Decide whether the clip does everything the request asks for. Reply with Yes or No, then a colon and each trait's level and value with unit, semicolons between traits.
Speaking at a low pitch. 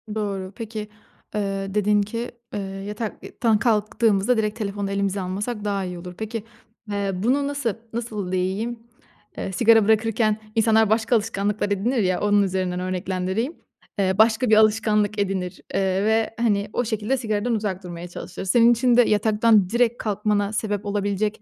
No: high, 210 Hz